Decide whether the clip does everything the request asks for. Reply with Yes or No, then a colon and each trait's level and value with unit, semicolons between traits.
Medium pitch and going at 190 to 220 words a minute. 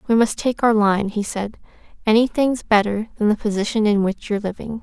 No: high, 215 Hz; average, 200 wpm